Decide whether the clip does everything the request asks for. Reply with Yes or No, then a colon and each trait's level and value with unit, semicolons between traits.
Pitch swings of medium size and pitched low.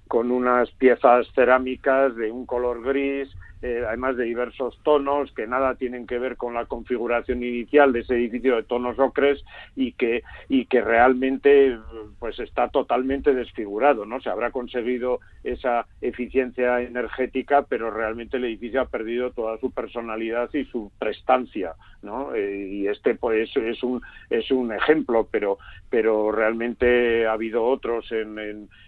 No: narrow, 2.2 semitones; low, 125 Hz